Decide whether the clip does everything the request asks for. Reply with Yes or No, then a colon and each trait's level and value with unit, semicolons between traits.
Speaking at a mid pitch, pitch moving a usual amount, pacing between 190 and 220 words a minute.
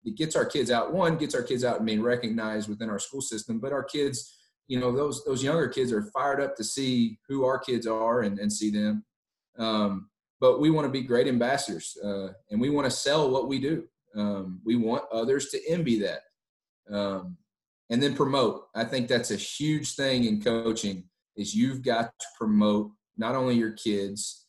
No: low, 115 Hz; average, 4.2 semitones; fast, 205 wpm